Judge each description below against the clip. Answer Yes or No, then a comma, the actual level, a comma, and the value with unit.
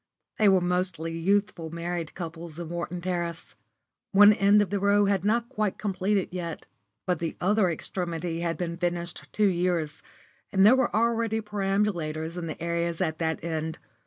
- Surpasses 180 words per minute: No, average, 165 wpm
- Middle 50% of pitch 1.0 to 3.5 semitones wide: Yes, average, 3.2 semitones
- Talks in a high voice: No, medium, 180 Hz